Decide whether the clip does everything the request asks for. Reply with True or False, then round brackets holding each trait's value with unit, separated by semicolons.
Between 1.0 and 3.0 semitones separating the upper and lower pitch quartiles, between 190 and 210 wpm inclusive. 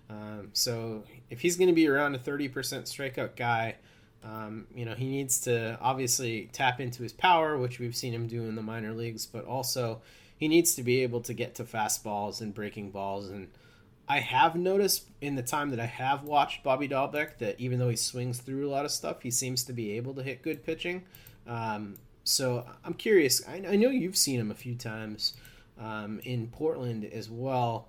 False (3.4 semitones; 205 wpm)